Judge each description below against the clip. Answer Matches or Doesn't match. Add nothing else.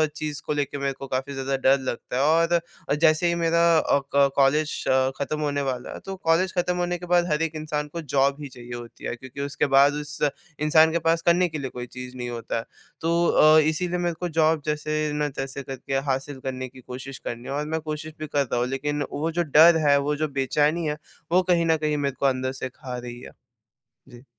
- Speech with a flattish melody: Doesn't match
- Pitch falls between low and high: Matches